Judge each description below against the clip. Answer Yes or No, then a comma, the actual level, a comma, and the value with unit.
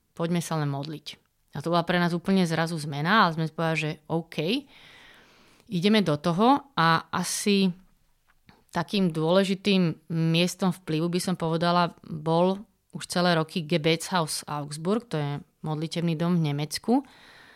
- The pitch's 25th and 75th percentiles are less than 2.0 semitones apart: No, average, 2.7 semitones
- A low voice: No, medium, 170 Hz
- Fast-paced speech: No, average, 140 wpm